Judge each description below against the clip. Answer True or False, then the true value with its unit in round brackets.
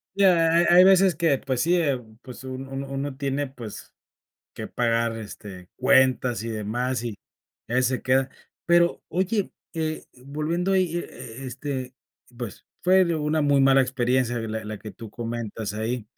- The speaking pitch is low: True (130 Hz)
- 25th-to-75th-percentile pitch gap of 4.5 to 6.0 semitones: True (5.0 semitones)